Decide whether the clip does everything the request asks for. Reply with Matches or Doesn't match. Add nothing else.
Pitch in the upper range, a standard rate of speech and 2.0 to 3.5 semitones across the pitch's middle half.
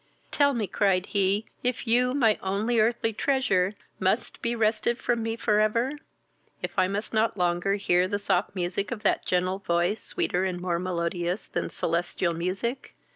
Doesn't match